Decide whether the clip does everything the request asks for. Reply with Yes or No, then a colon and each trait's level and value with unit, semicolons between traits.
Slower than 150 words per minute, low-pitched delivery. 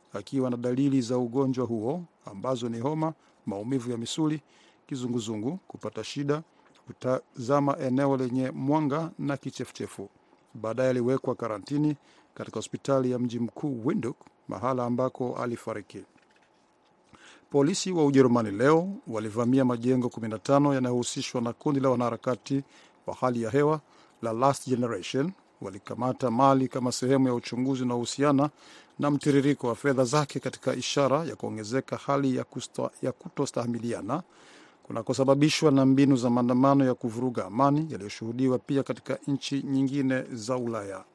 Yes: average, 130 wpm; low, 130 Hz